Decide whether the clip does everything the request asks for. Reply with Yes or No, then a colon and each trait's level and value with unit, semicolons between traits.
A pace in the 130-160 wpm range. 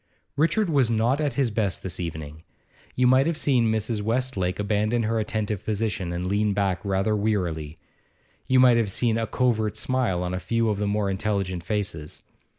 No: average, 180 wpm